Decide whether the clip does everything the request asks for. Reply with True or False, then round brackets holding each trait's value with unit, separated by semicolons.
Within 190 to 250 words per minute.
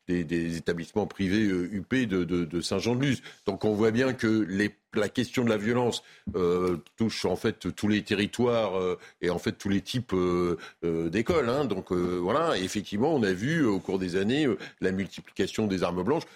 True (205 wpm)